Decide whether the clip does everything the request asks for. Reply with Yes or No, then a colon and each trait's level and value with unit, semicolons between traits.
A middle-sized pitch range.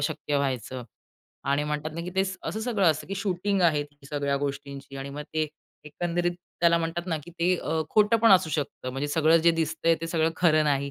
Yes: average, 3.4 semitones